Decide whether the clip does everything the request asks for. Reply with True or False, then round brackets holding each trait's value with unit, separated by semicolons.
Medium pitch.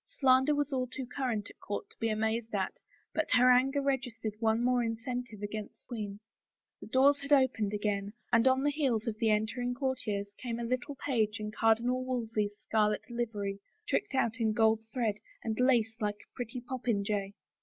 False (230 Hz)